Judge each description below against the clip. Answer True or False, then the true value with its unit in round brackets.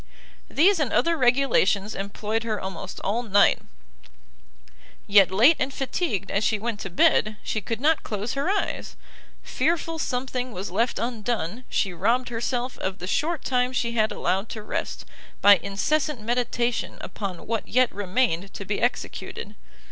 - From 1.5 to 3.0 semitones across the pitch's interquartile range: False (4.1 semitones)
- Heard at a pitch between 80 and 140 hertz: False (230 Hz)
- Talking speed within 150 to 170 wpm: True (155 wpm)